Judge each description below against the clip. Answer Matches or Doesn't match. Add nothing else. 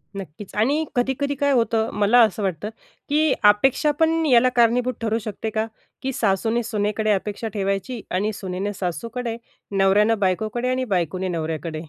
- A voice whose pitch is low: Doesn't match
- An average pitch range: Matches